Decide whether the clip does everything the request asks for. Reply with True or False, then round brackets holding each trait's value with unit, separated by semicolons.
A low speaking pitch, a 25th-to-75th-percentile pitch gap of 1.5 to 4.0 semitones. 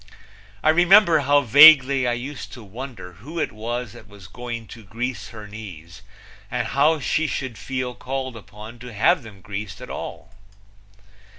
False (120 Hz; 4.7 semitones)